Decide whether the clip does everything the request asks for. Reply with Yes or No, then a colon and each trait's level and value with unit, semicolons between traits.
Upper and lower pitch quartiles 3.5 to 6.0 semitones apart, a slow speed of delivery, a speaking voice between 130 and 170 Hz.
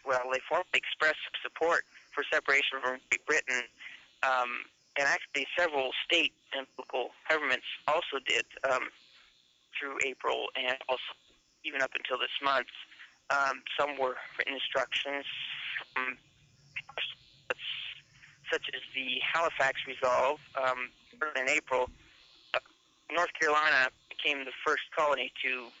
No: narrow, 2.6 semitones; slow, 120 wpm; low, 135 Hz